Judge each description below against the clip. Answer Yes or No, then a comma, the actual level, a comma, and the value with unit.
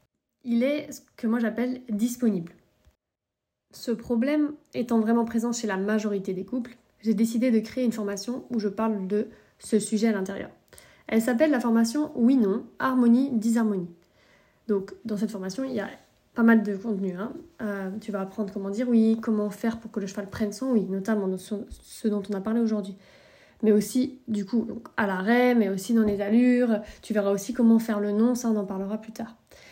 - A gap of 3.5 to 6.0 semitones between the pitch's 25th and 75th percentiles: No, average, 2.7 semitones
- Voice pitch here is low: No, high, 225 Hz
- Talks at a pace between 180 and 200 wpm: Yes, average, 195 wpm